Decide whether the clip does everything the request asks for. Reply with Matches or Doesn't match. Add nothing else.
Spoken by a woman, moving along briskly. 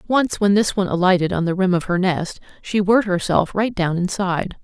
Matches